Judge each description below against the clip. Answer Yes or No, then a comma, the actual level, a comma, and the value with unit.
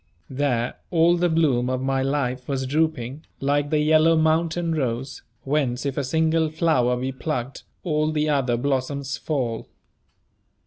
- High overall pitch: No, medium, 145 Hz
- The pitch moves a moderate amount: Yes, average, 3.5 semitones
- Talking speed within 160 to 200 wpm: No, average, 145 wpm